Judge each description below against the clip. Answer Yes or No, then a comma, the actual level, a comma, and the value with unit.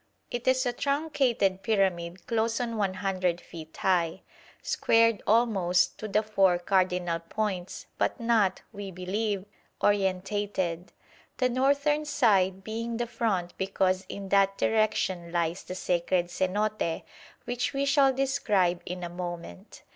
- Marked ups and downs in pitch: No, average, 4.1 semitones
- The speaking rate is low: Yes, slow, 130 wpm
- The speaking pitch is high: Yes, high, 195 Hz